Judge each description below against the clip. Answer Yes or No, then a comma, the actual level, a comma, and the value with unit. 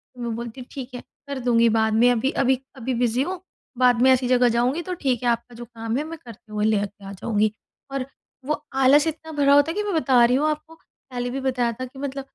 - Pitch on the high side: Yes, very high, 250 Hz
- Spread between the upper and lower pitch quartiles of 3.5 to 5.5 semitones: No, average, 3.0 semitones